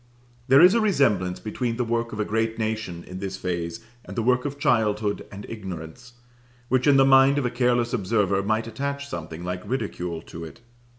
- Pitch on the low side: Yes, low, 110 Hz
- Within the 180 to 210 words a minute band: Yes, average, 195 wpm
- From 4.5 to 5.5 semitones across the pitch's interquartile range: Yes, average, 4.9 semitones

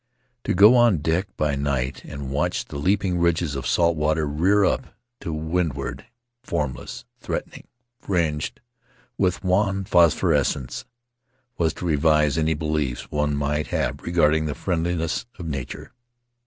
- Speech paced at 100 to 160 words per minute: Yes, average, 145 wpm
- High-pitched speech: No, very low, 80 Hz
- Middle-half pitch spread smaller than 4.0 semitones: Yes, average, 3.6 semitones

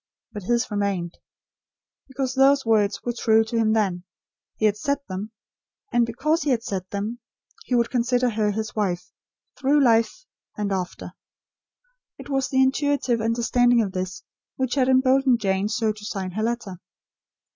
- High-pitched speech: Yes, high, 225 Hz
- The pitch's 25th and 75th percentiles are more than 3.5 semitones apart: Yes, average, 3.9 semitones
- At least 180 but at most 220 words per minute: No, average, 160 wpm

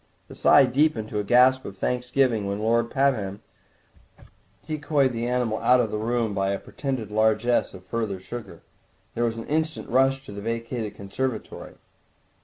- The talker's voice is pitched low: Yes, low, 115 Hz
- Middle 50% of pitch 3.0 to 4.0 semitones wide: Yes, average, 3.6 semitones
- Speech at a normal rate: Yes, average, 170 wpm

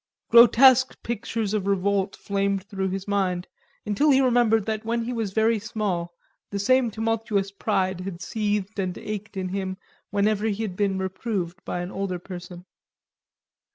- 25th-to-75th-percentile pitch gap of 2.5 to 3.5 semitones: Yes, average, 2.8 semitones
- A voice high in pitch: Yes, high, 200 Hz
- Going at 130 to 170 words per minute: Yes, average, 155 wpm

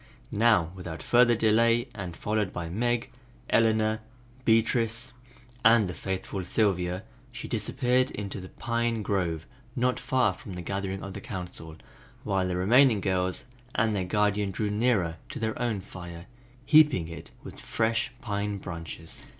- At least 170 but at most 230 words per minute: No, average, 145 wpm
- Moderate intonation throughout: Yes, average, 4.1 semitones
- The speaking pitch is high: No, low, 105 Hz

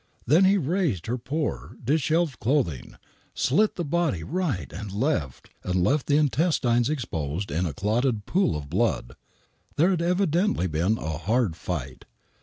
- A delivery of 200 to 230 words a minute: No, average, 155 wpm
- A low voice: Yes, low, 125 Hz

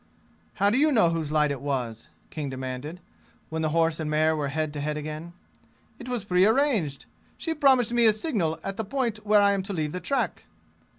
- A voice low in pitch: No, medium, 165 Hz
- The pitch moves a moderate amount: No, wide, 6.3 semitones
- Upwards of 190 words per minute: Yes, fast, 205 wpm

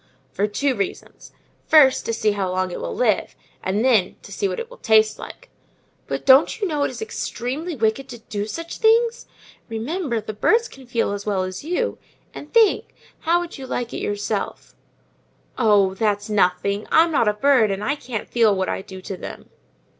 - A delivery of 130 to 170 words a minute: No, average, 190 wpm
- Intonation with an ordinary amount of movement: No, wide, 6.7 semitones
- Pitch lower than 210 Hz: No, high, 230 Hz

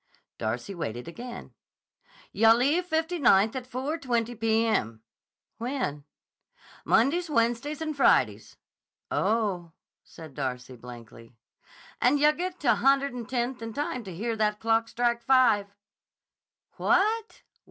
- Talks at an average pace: No, slow, 120 wpm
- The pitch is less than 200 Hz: No, high, 235 Hz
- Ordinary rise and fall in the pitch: No, wide, 5.9 semitones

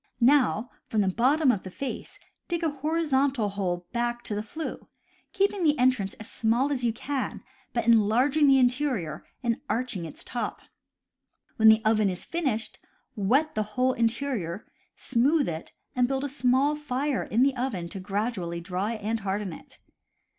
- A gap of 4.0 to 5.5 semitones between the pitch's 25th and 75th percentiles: Yes, average, 4.7 semitones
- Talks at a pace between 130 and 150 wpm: No, average, 165 wpm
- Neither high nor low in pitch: No, high, 240 Hz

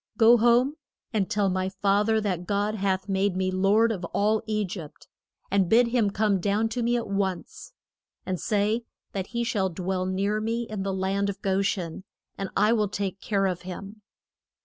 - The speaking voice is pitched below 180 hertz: No, high, 200 Hz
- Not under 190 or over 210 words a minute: Yes, average, 195 wpm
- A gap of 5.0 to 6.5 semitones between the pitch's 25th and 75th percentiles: No, narrow, 2.4 semitones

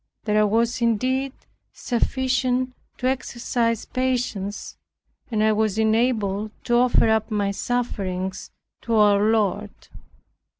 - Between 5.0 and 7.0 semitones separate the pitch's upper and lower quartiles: No, average, 2.9 semitones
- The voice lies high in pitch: Yes, high, 225 Hz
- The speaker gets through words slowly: Yes, slow, 110 wpm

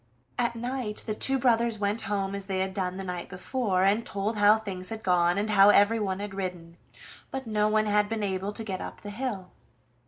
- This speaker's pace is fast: Yes, fast, 215 wpm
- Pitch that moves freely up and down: No, narrow, 2.5 semitones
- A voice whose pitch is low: No, high, 205 Hz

